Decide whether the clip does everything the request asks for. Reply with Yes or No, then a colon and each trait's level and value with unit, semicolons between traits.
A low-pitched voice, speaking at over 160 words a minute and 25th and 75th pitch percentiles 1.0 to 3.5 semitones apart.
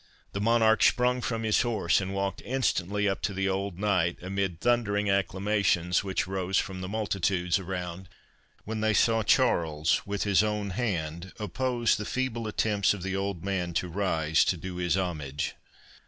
Yes: low, 100 Hz; average, 170 wpm; average, 3.0 semitones